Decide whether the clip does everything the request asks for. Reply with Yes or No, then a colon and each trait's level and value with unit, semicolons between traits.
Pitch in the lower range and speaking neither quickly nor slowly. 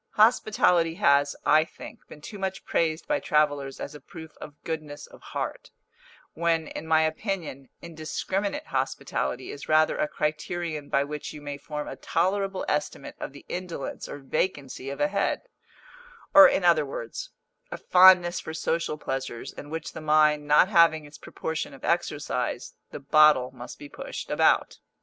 No: medium, 155 Hz; average, 165 wpm